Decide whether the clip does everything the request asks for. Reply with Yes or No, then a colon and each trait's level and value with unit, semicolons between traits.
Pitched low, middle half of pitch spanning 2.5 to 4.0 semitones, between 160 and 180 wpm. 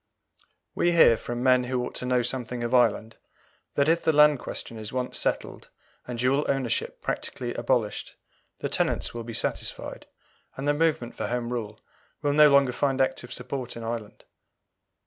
Yes: low, 125 Hz; average, 2.8 semitones; average, 170 wpm